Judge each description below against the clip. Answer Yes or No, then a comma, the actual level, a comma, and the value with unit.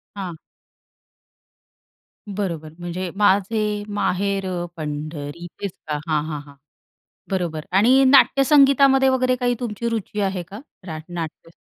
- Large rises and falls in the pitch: Yes, wide, 6.0 semitones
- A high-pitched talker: Yes, high, 195 Hz